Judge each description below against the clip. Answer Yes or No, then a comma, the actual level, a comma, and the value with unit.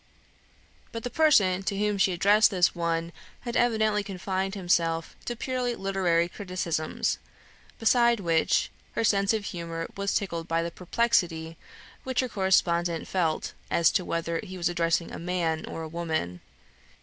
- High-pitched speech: No, medium, 180 Hz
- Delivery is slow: No, average, 150 wpm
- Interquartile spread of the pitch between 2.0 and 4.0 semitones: Yes, average, 3.7 semitones